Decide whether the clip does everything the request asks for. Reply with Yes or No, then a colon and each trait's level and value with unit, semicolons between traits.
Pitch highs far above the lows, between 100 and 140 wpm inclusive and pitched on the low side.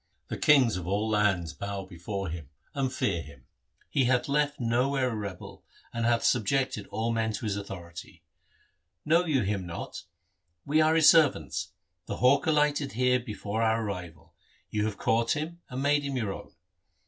No: wide, 5.7 semitones; average, 170 wpm; low, 115 Hz